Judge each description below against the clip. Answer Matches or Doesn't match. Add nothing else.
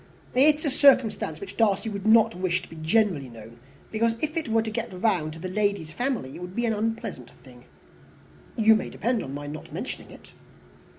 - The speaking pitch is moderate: Doesn't match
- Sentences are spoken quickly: Matches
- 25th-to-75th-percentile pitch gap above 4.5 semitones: Matches